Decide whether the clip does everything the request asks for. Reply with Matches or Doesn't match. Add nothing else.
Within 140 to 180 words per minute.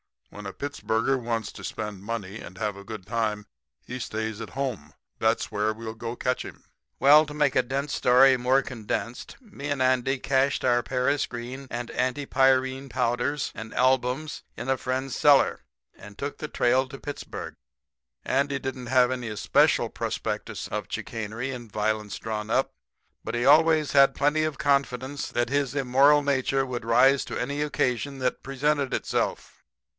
Matches